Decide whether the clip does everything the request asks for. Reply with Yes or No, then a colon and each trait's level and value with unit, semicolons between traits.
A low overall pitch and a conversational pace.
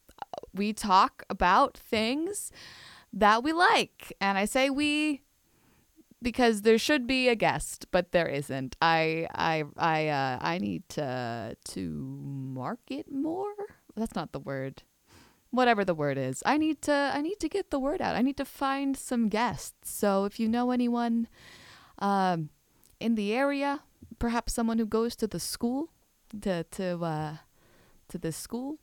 No: high, 225 Hz; average, 160 wpm